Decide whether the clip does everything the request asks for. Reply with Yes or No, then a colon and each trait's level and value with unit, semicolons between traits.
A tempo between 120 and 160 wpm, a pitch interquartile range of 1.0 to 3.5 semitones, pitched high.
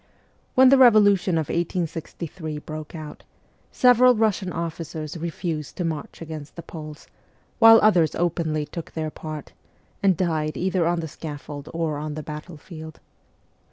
No: average, 140 wpm; average, 2.9 semitones; medium, 165 Hz